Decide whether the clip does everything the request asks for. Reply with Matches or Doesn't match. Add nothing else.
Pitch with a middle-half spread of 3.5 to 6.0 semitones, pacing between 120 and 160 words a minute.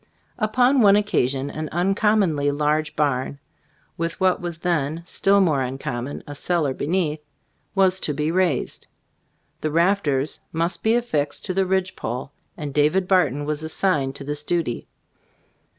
Matches